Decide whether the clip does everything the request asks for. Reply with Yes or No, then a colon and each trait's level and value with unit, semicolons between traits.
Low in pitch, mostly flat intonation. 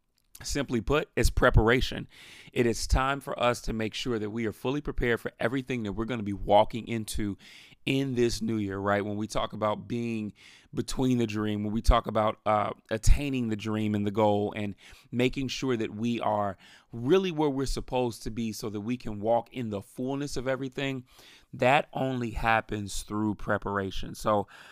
No: low, 115 Hz; average, 3.3 semitones